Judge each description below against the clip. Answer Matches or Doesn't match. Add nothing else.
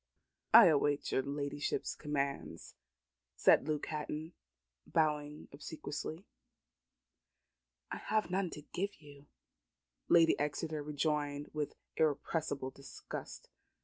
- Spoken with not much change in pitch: Matches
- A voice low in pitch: Doesn't match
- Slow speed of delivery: Matches